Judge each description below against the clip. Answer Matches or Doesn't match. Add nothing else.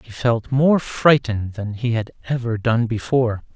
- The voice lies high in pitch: Doesn't match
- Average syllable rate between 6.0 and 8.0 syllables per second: Doesn't match